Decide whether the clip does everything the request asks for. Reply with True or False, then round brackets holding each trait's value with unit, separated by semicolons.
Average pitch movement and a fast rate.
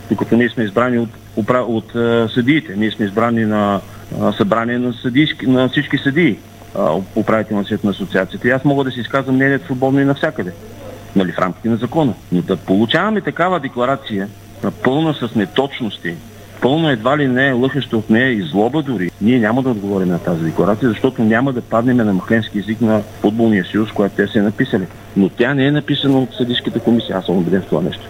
True (4.1 semitones; 195 wpm)